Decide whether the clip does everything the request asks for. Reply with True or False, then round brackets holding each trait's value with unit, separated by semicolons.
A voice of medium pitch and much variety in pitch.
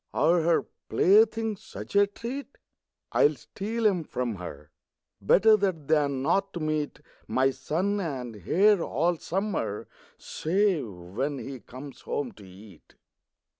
True (155 Hz; 7.4 semitones)